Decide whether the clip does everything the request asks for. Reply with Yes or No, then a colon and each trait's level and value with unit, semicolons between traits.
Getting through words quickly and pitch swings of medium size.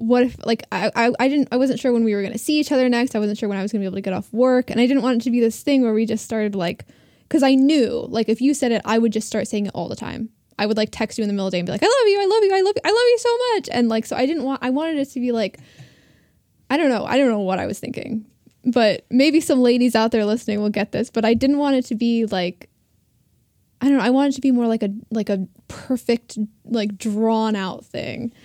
Yes: fast, 315 wpm; average, 3.6 semitones